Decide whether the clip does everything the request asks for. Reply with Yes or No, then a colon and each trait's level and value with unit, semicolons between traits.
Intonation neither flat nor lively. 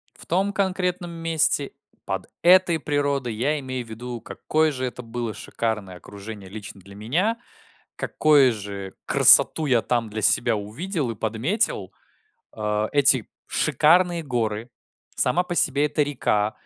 No: wide, 6.5 semitones